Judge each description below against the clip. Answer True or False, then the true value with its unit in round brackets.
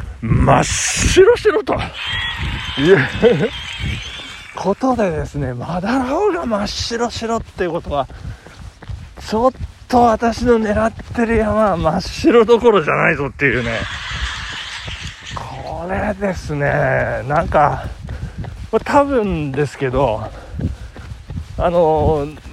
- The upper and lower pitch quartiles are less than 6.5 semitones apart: False (7.9 semitones)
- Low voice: False (215 Hz)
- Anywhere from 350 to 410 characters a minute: False (195 characters per minute)